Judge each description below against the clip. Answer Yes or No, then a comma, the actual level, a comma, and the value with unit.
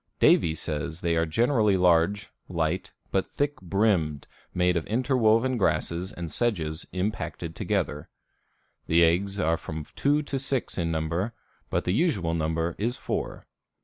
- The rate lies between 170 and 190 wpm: No, average, 145 wpm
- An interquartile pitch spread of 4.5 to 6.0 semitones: Yes, average, 5.1 semitones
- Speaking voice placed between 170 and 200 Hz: No, very low, 90 Hz